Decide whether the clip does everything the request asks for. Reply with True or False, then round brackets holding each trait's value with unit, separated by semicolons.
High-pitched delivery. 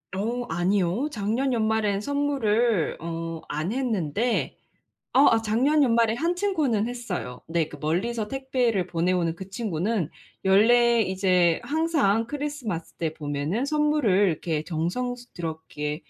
True (210 Hz)